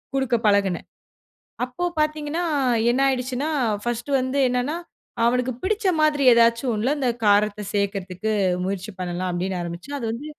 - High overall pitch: Yes, high, 240 Hz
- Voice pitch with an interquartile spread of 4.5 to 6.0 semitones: Yes, wide, 5.5 semitones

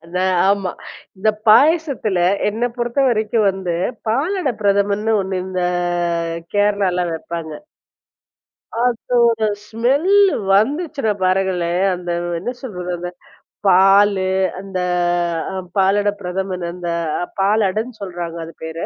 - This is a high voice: Yes, high, 200 Hz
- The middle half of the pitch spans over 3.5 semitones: Yes, average, 4.1 semitones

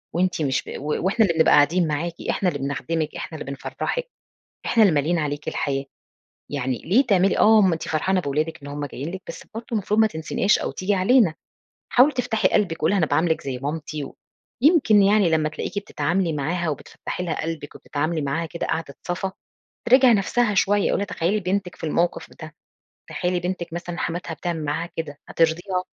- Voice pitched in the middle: Yes, medium, 170 Hz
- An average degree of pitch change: Yes, average, 4.3 semitones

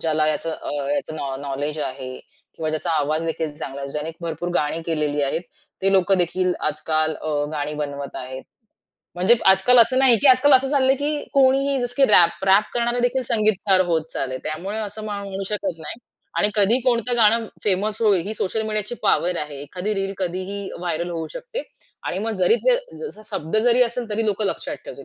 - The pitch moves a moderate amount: No, wide, 6.3 semitones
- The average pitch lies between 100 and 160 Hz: No, high, 190 Hz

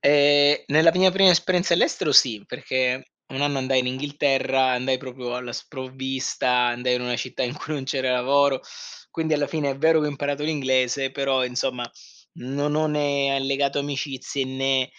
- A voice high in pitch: No, low, 135 Hz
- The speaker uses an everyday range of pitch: No, narrow, 2.0 semitones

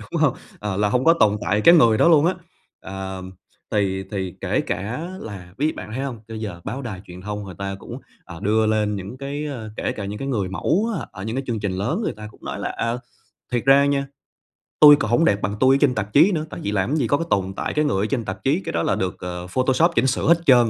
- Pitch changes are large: Yes, wide, 5.9 semitones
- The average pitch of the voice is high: No, low, 110 Hz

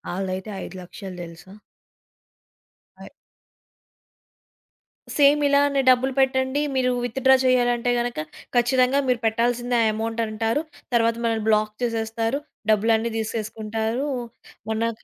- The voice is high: Yes, high, 230 Hz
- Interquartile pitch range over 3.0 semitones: No, narrow, 2.6 semitones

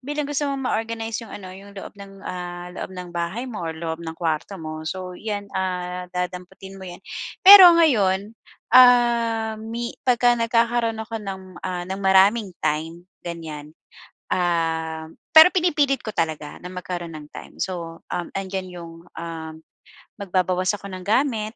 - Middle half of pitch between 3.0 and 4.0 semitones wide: No, average, 4.7 semitones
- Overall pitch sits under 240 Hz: Yes, high, 190 Hz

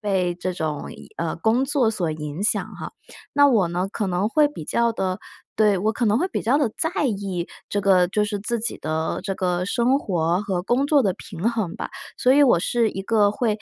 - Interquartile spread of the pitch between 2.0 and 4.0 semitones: No, average, 4.7 semitones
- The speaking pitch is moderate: No, high, 205 Hz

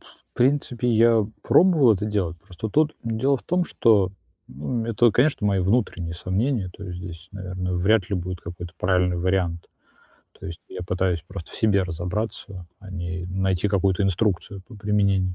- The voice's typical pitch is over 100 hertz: No, very low, 95 Hz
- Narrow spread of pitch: No, average, 3.7 semitones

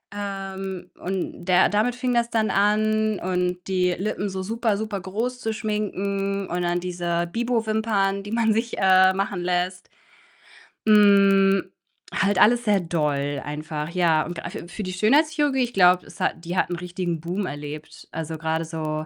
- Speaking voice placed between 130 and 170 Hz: No, high, 190 Hz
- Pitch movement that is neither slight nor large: Yes, average, 3.4 semitones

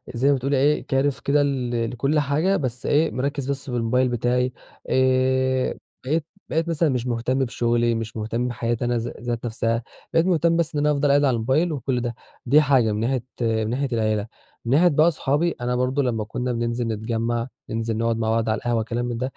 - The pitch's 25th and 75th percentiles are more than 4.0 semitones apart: No, average, 3.3 semitones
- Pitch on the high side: No, low, 125 Hz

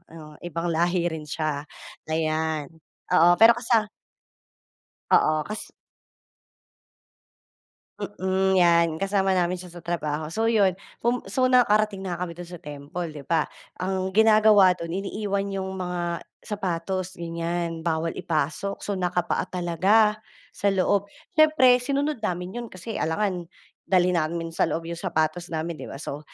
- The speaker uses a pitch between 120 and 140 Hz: No, medium, 180 Hz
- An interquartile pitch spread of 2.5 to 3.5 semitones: Yes, average, 3.2 semitones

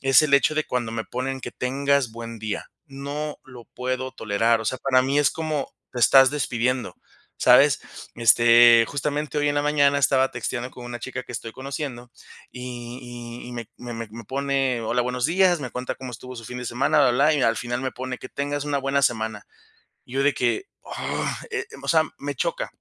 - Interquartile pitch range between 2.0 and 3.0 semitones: Yes, average, 2.7 semitones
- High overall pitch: No, low, 130 Hz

